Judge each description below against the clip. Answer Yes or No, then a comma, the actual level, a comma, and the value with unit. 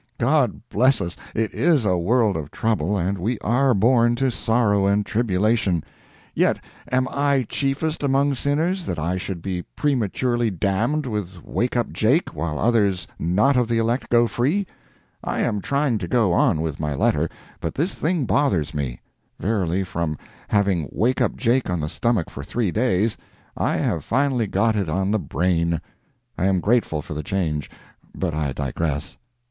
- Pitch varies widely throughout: Yes, wide, 6.3 semitones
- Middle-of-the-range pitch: No, low, 105 Hz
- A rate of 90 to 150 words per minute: No, average, 170 wpm